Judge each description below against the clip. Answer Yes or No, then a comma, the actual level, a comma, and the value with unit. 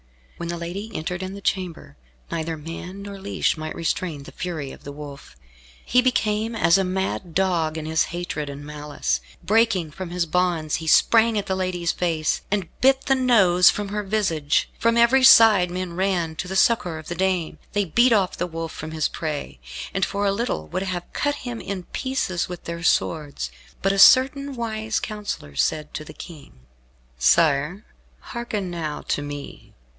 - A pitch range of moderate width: Yes, average, 4.5 semitones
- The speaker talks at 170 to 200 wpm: Yes, average, 185 wpm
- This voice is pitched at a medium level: Yes, medium, 180 Hz